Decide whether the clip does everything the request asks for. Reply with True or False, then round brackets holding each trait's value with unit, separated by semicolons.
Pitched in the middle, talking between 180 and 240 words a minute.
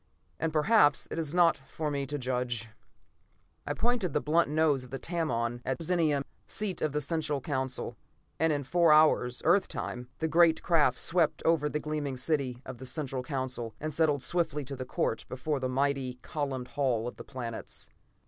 True (145 Hz; 185 wpm)